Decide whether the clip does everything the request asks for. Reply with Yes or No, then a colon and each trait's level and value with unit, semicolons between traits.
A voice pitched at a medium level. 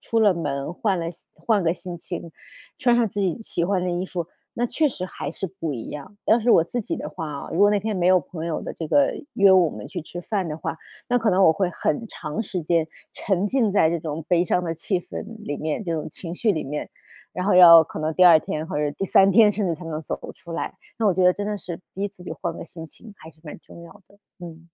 Yes: medium, 175 Hz